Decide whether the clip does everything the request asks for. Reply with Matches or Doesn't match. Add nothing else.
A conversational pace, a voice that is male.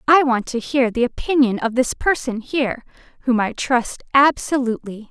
Doesn't match